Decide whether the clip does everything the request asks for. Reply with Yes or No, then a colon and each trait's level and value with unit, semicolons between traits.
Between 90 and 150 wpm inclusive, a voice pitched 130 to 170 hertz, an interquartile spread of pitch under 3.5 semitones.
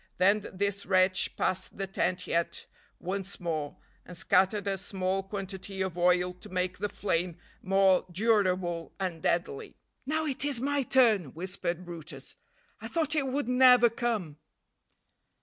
No: average, 145 wpm; high, 190 Hz; average, 2.9 semitones